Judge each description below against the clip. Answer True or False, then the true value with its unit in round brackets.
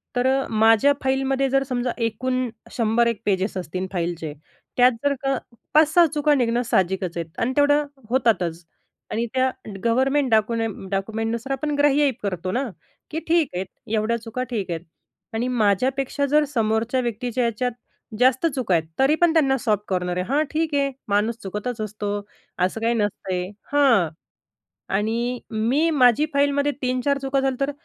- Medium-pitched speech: False (240 Hz)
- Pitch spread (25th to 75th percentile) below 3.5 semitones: False (4.5 semitones)